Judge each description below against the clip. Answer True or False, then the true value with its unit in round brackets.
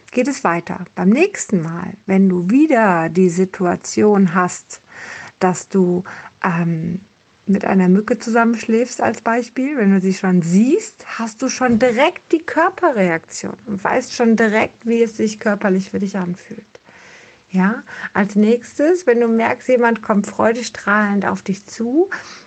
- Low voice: False (215 Hz)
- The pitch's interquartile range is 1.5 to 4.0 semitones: False (4.4 semitones)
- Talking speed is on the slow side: False (145 wpm)